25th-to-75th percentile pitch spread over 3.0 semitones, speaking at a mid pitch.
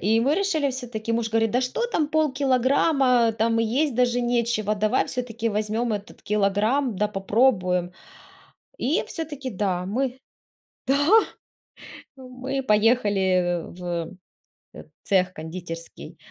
No: average, 4.3 semitones; high, 230 Hz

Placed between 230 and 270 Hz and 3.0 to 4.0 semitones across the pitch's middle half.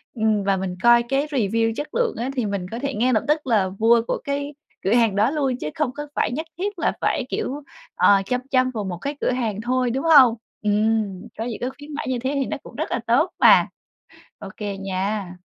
No: high, 240 Hz; average, 4.7 semitones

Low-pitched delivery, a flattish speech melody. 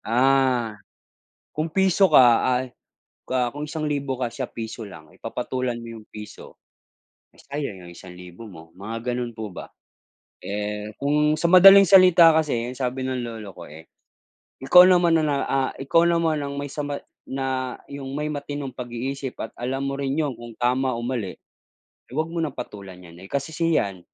No: low, 130 Hz; average, 4.4 semitones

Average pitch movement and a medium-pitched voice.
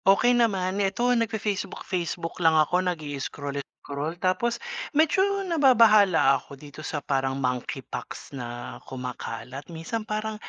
No: wide, 7.3 semitones; medium, 175 Hz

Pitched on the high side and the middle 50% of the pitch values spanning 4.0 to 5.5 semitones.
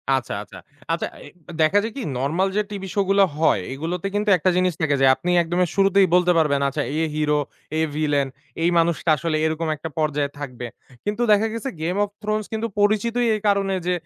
No: medium, 175 Hz; average, 4.9 semitones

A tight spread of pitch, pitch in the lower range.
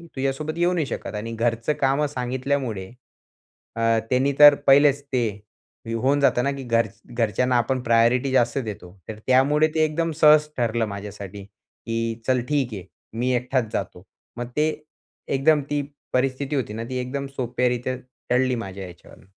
No: average, 3.4 semitones; low, 125 Hz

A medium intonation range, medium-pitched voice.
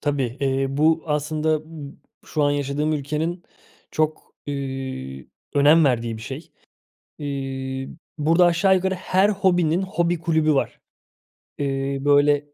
Yes: average, 3.2 semitones; medium, 150 Hz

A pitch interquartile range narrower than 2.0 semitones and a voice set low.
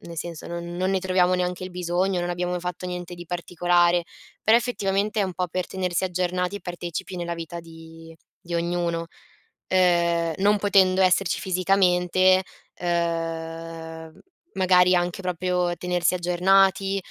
No: narrow, 1.3 semitones; medium, 180 Hz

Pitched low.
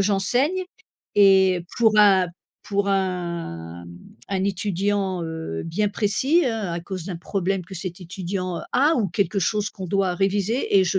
No: high, 195 Hz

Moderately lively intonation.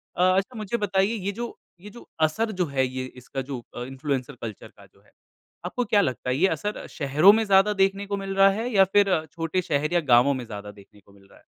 No: wide, 7.3 semitones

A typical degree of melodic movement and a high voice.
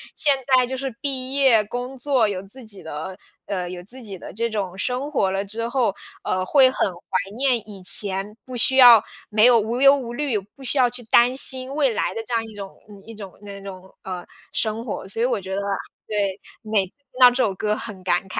Yes: average, 4.6 semitones; high, 225 Hz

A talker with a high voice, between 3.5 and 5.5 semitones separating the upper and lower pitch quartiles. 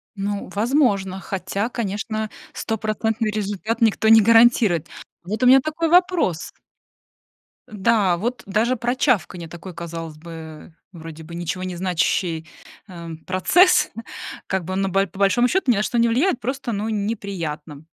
Yes: high, 200 Hz; average, 4.9 semitones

